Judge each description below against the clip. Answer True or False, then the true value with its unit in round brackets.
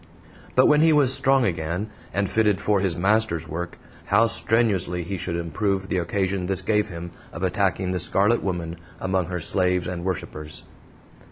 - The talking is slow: False (170 wpm)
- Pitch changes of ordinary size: True (3.3 semitones)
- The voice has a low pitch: True (95 Hz)